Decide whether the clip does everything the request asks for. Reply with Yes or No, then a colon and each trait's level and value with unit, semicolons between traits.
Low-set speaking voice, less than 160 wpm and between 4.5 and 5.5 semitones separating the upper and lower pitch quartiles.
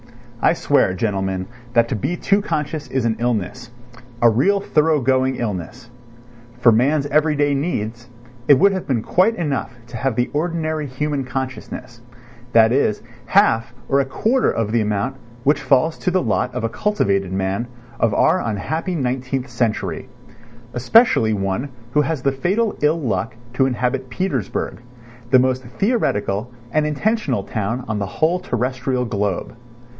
Yes: low, 130 Hz; average, 150 wpm; average, 4.8 semitones